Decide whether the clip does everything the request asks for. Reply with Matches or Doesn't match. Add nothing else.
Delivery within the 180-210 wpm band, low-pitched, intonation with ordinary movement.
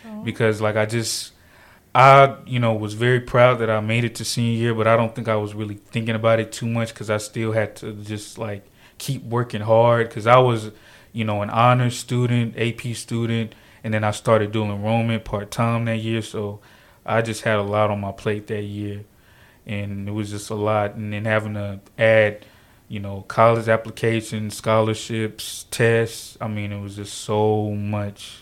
Doesn't match